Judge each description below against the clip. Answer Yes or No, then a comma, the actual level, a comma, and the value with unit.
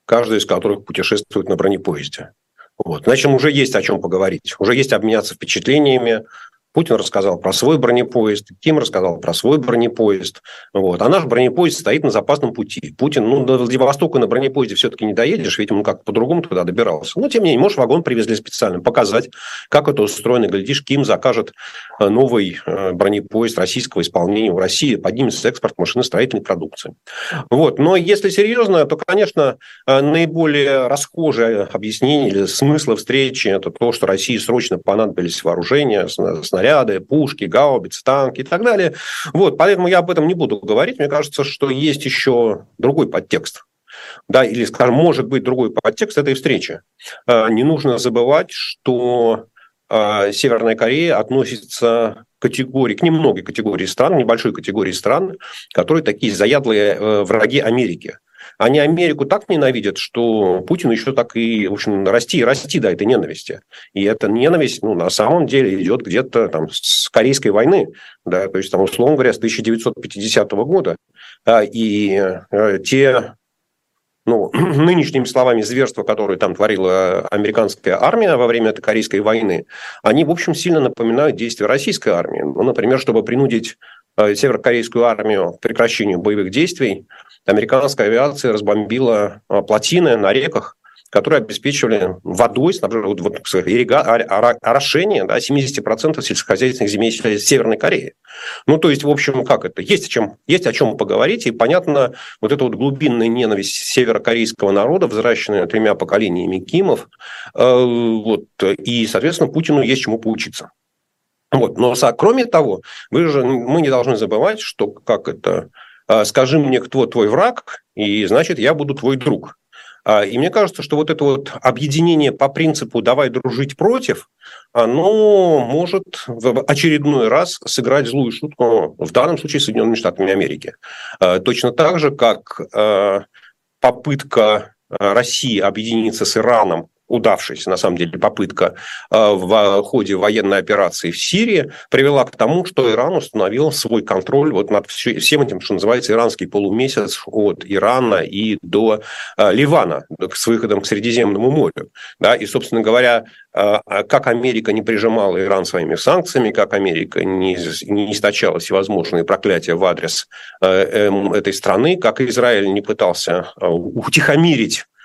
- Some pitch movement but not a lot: Yes, average, 4.8 semitones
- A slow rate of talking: No, average, 145 wpm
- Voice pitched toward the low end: Yes, low, 120 Hz